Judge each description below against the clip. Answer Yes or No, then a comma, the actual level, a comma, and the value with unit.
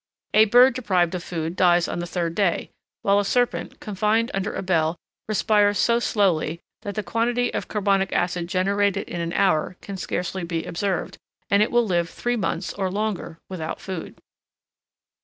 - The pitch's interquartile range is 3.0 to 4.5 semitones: Yes, average, 3.3 semitones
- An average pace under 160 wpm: No, average, 175 wpm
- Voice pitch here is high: Yes, high, 195 Hz